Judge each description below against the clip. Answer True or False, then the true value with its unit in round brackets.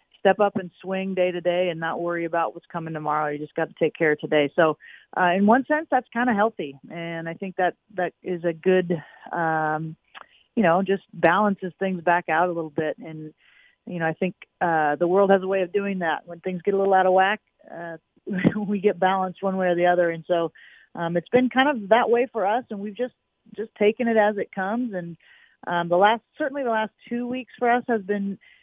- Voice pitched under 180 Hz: False (185 Hz)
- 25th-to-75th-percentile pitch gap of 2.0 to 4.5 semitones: True (3.8 semitones)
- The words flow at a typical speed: False (240 wpm)